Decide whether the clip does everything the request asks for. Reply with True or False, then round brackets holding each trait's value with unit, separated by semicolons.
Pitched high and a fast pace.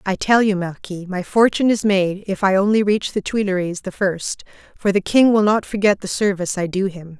True (195 Hz; 225 wpm)